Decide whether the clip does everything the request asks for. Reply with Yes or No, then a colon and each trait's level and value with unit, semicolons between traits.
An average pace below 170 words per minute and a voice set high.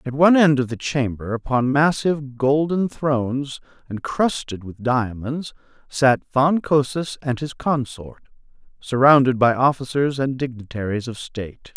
No: slow, 135 wpm; low, 135 Hz